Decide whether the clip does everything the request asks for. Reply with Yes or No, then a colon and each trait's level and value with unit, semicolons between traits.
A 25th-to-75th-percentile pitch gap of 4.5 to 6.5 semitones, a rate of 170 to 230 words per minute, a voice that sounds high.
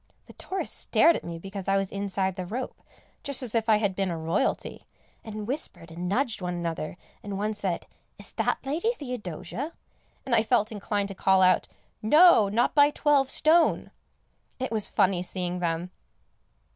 Yes: wide, 5.6 semitones; average, 175 wpm; high, 205 Hz